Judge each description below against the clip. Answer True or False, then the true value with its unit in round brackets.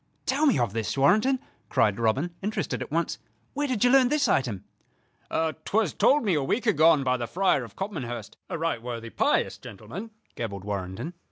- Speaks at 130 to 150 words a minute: False (185 wpm)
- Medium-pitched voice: True (150 Hz)